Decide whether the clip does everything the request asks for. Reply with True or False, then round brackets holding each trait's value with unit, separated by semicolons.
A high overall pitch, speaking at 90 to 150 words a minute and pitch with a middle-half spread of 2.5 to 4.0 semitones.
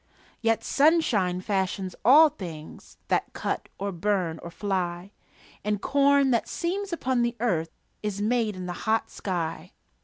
False (205 Hz; 145 wpm; 5.4 semitones)